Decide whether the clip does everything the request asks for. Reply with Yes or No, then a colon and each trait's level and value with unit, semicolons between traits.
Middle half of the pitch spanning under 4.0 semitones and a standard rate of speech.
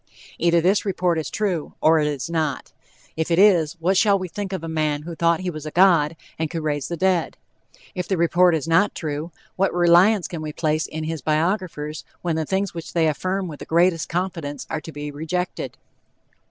No: average, 2.7 semitones; fast, 210 wpm